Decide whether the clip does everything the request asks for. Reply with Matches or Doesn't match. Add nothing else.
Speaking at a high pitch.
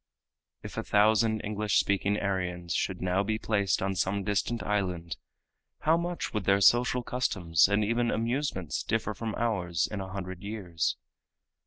Doesn't match